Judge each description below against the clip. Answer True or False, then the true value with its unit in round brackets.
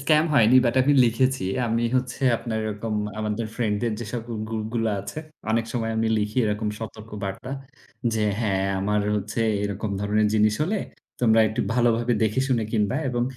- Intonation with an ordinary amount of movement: False (2.2 semitones)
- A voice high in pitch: False (110 Hz)